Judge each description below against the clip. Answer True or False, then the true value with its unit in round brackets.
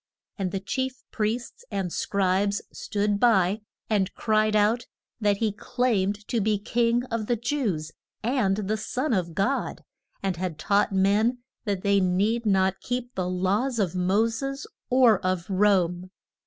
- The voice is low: False (205 Hz)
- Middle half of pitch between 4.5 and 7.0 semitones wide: False (3.4 semitones)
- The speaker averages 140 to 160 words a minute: True (155 wpm)